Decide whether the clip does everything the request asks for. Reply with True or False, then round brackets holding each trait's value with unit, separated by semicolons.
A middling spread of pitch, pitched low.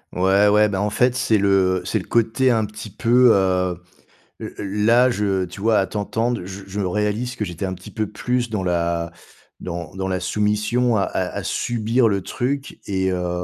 True (3.5 semitones; 105 Hz)